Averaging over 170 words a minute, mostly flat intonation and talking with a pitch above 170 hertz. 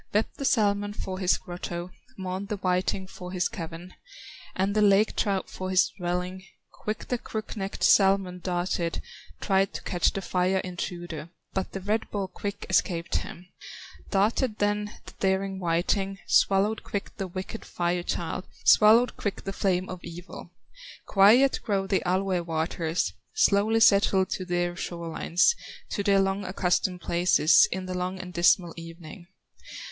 No: average, 155 wpm; narrow, 2.2 semitones; high, 190 Hz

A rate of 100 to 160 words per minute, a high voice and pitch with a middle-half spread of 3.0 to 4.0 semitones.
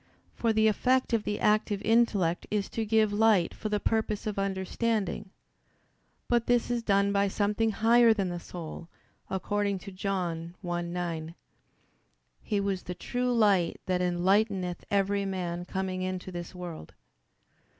Yes: average, 145 wpm; high, 200 Hz; average, 3.3 semitones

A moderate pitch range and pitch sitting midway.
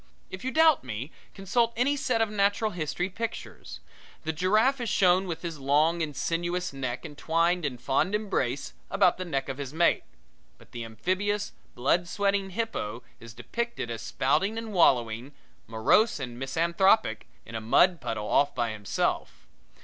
No: wide, 7.3 semitones; medium, 170 Hz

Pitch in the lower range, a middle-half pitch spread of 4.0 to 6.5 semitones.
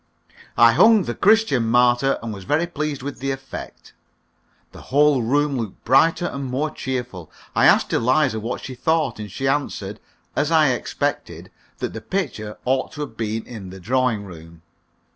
Yes: low, 130 Hz; average, 4.6 semitones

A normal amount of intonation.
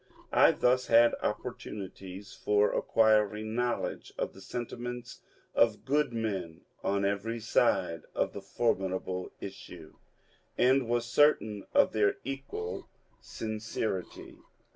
Yes: average, 3.3 semitones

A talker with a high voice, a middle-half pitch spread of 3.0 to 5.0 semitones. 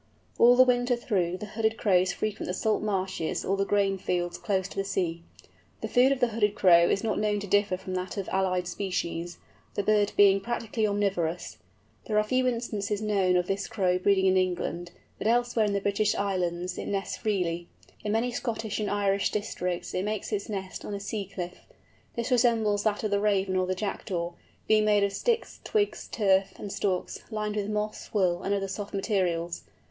No: high, 200 Hz; narrow, 2.5 semitones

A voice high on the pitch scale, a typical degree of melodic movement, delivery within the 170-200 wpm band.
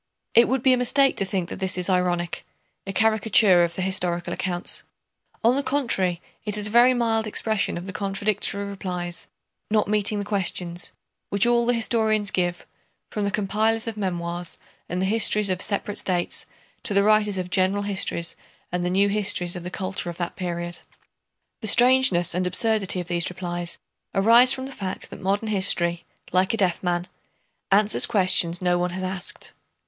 Yes: high, 195 Hz; average, 3.4 semitones; average, 180 wpm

